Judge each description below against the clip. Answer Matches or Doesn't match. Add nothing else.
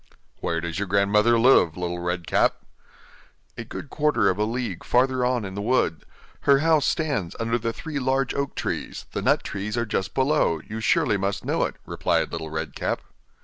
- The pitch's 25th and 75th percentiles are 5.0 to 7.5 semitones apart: Matches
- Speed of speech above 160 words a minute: Matches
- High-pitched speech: Doesn't match